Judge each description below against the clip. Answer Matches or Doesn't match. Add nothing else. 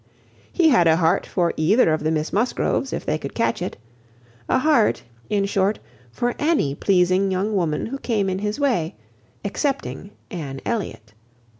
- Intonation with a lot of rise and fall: Matches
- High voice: Matches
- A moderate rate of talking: Matches